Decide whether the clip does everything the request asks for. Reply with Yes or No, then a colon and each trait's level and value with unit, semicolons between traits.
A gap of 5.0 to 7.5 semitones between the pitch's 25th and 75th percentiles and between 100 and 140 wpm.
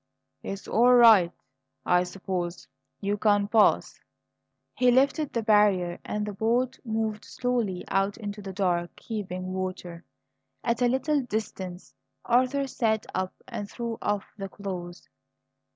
No: average, 3.9 semitones; slow, 135 wpm